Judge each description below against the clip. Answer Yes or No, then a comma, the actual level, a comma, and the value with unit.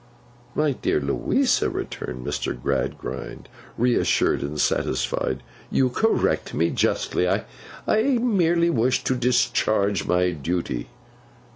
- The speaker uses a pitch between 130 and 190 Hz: No, low, 110 Hz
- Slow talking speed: Yes, slow, 105 wpm